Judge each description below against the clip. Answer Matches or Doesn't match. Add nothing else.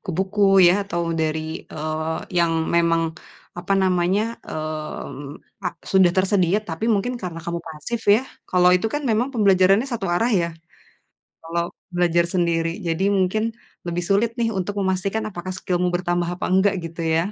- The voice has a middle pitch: Matches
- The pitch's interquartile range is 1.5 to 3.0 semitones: Matches